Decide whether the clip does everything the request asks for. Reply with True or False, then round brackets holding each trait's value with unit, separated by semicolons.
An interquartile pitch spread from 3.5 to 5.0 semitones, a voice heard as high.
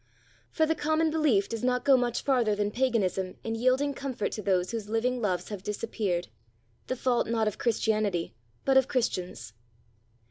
True (3.9 semitones; 230 Hz)